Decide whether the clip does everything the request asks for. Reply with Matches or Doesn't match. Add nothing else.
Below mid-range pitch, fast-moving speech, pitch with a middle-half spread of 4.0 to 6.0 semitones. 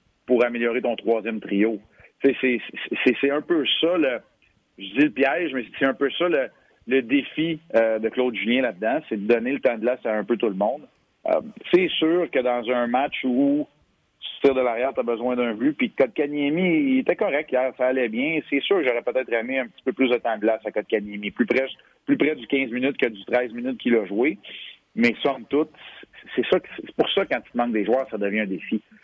Matches